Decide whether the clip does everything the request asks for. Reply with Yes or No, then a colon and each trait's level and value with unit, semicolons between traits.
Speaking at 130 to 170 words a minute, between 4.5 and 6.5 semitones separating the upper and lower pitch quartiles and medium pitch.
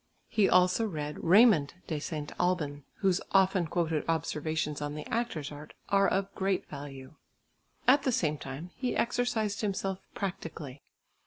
Yes: average, 145 wpm; average, 4.8 semitones; medium, 170 Hz